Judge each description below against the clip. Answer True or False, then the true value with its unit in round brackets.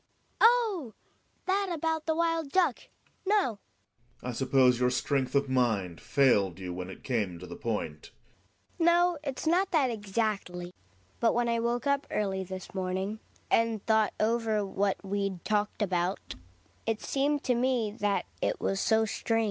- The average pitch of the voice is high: True (210 Hz)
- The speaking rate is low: False (160 wpm)